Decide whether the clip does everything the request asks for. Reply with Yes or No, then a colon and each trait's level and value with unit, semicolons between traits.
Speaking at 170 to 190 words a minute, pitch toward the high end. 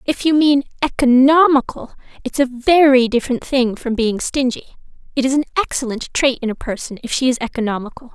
Yes: average, 175 wpm; very high, 260 Hz